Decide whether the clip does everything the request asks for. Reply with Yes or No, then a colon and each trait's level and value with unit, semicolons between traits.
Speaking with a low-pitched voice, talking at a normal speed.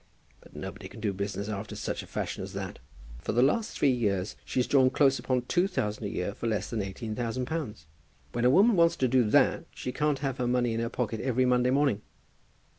No: low, 120 Hz; fast, 225 wpm